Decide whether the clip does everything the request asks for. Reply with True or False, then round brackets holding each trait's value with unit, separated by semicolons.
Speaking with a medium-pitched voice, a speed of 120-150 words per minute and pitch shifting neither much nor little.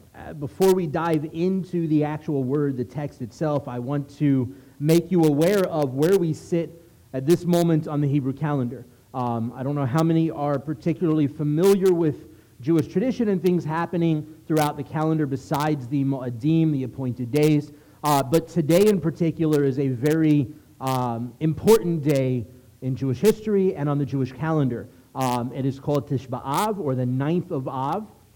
False (150 Hz; 175 wpm; 3.6 semitones)